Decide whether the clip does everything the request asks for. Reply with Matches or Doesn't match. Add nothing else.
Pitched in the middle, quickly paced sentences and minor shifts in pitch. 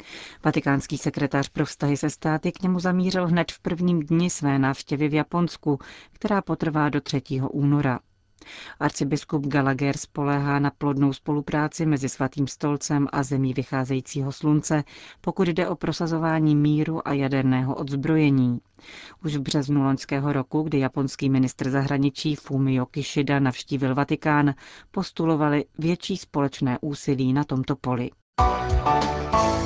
Doesn't match